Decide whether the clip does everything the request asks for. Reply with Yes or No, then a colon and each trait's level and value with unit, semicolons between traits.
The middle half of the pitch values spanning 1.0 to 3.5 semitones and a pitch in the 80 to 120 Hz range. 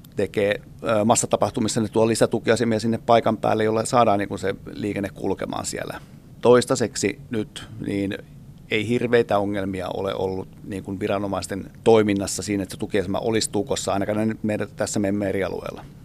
Yes: narrow, 2.6 semitones; low, 110 Hz